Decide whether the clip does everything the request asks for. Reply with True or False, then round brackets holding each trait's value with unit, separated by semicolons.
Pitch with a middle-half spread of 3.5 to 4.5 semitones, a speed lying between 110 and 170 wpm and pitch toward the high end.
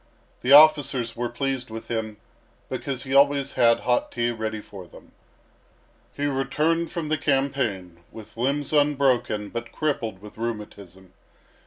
False (4.2 semitones; 140 wpm; 125 Hz)